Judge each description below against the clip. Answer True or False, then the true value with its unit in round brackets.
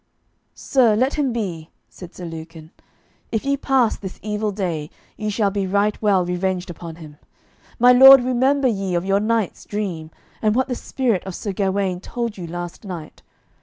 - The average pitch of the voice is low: False (200 Hz)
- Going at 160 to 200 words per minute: True (175 wpm)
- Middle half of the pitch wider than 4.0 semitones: True (4.8 semitones)